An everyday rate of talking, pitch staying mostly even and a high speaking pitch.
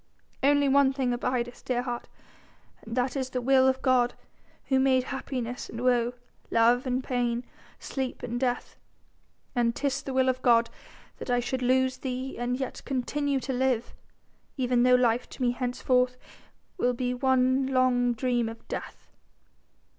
Yes: average, 160 wpm; narrow, 1.3 semitones; very high, 250 Hz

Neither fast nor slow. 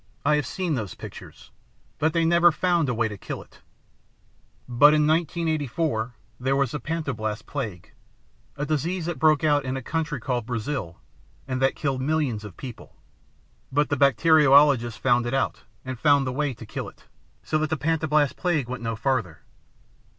Yes: average, 175 wpm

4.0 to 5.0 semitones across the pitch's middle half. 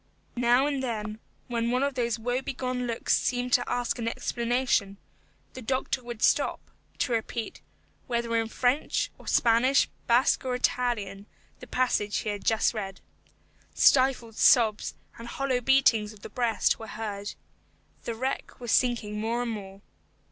No: narrow, 2.4 semitones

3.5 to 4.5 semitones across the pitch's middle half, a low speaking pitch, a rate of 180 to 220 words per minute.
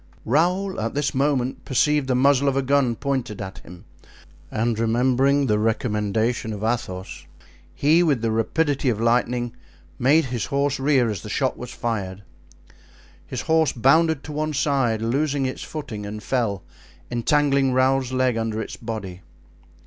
No: average, 3.8 semitones; low, 125 Hz; average, 155 wpm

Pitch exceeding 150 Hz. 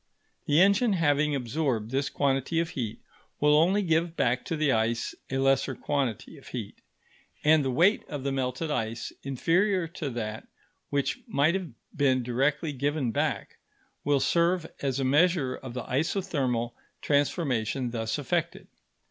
No: medium, 140 Hz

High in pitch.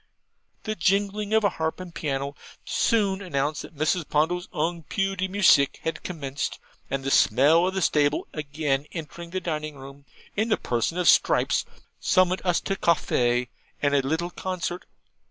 No: medium, 165 Hz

